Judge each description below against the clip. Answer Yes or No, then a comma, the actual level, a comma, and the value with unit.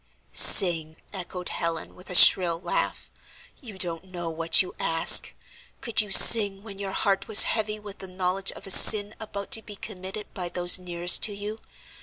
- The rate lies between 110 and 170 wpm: No, average, 180 wpm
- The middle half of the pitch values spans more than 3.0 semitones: No, average, 2.7 semitones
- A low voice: No, high, 190 Hz